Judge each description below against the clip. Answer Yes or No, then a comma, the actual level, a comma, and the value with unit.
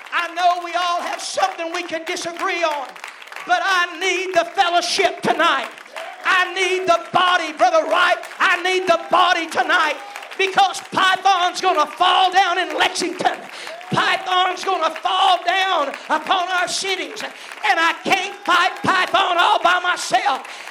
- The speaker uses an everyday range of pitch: No, narrow, 1.3 semitones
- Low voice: No, very high, 360 Hz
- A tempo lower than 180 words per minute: Yes, average, 140 wpm